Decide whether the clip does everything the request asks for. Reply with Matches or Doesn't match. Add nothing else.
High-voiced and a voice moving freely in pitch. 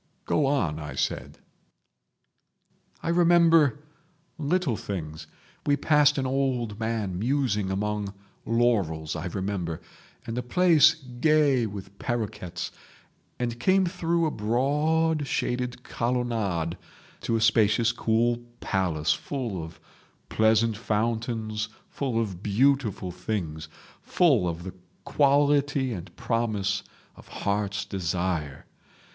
Doesn't match